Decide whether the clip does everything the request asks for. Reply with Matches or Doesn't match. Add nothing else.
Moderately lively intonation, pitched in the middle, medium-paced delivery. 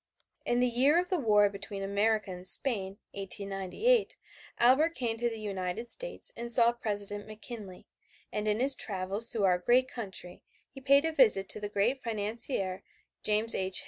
Doesn't match